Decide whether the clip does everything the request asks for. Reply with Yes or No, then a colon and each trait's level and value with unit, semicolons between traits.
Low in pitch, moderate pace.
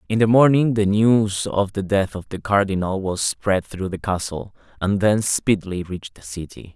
Yes: low, 100 Hz; average, 195 wpm